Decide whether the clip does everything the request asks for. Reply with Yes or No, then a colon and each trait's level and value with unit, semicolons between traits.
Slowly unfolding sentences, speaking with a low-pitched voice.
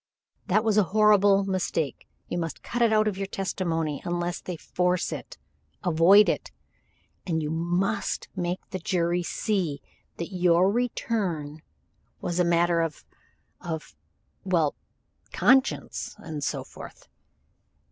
No: slow, 130 wpm; medium, 180 Hz